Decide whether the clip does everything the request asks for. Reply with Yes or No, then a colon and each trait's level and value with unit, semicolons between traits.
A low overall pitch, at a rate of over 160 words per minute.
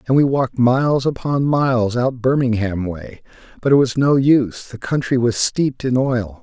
Yes: low, 125 Hz; average, 185 wpm